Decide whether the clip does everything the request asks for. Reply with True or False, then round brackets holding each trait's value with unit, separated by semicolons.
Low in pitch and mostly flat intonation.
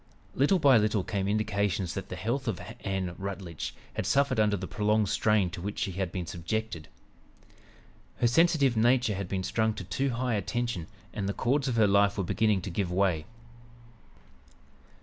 False (105 Hz; 3.7 semitones)